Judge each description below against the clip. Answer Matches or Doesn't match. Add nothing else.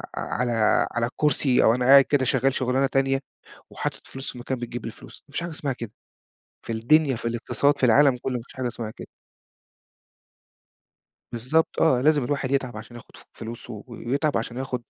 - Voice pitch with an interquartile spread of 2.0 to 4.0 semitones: Matches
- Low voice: Matches